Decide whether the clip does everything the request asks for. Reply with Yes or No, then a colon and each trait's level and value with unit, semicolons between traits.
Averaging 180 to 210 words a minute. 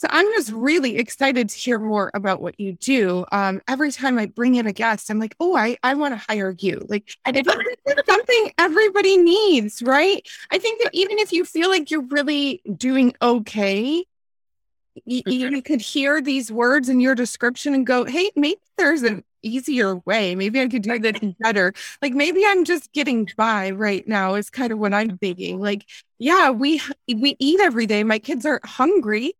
Yes: average, 195 wpm